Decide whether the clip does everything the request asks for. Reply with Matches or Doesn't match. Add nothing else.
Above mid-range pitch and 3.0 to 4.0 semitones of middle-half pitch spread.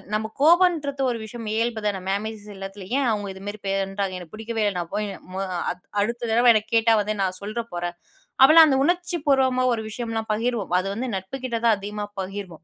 Matches